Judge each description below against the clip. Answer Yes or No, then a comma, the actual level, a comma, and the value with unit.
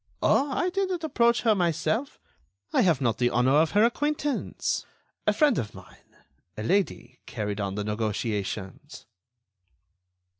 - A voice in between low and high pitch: Yes, medium, 155 Hz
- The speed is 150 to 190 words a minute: No, average, 140 wpm